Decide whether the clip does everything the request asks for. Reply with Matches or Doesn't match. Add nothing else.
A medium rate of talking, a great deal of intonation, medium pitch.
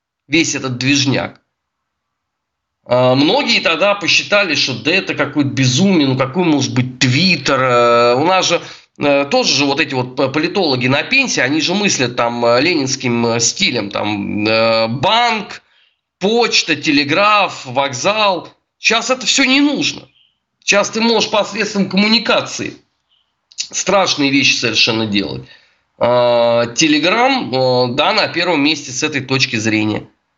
Matches